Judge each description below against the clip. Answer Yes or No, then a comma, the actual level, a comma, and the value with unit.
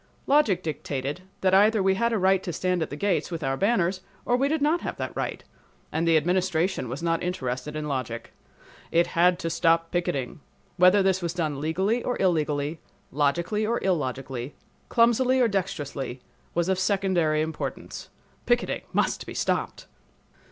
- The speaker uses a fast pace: No, average, 165 wpm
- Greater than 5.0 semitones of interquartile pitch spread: No, average, 4.3 semitones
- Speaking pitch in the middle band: Yes, medium, 175 Hz